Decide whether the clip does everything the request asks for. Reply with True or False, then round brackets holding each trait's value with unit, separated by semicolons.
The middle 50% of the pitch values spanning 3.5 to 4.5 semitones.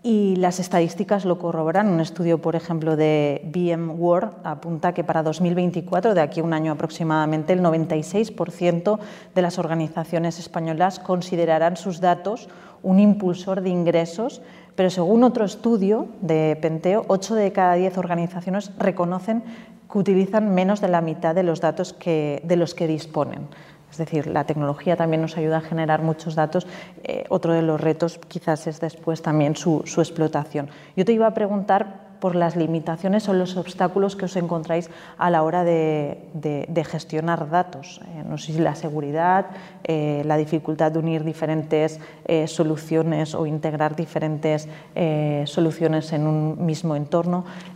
False (2.6 semitones)